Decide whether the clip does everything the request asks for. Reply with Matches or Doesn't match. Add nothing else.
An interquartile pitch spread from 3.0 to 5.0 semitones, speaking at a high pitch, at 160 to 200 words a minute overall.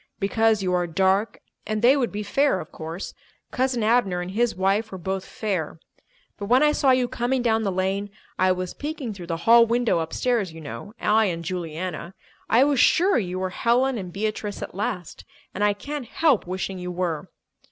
Matches